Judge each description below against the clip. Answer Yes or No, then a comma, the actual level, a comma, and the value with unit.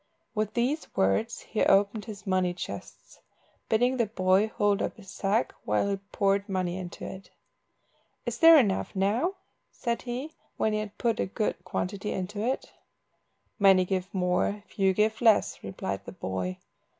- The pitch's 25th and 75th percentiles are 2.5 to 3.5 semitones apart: Yes, average, 3.0 semitones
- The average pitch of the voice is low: No, high, 200 Hz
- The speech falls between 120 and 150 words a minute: No, average, 160 wpm